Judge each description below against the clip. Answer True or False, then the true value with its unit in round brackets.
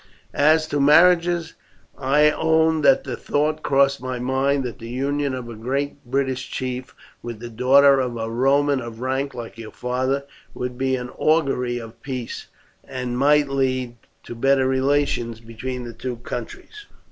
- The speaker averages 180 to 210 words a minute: False (160 wpm)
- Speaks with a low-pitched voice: True (130 Hz)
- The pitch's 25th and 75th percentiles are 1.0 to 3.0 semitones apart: True (2.7 semitones)